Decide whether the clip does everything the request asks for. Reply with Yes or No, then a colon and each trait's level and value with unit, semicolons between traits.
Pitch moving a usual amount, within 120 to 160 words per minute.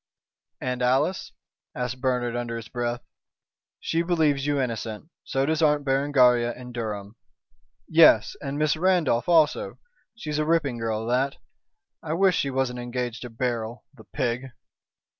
Yes: average, 3.7 semitones; average, 140 wpm